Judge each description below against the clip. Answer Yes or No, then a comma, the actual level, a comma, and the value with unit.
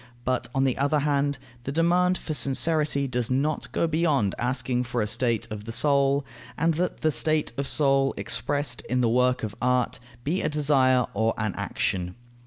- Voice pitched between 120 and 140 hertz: Yes, low, 135 Hz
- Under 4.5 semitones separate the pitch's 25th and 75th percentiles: Yes, average, 3.5 semitones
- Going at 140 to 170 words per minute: No, average, 185 wpm